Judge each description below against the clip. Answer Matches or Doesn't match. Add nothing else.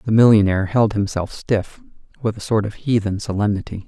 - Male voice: Matches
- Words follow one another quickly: Doesn't match